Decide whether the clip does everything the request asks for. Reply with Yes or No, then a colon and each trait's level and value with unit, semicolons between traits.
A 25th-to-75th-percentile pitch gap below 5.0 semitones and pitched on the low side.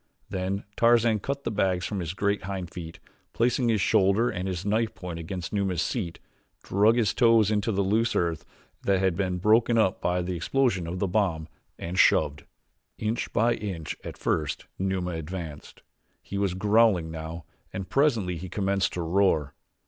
Yes: average, 3.5 semitones; very low, 95 Hz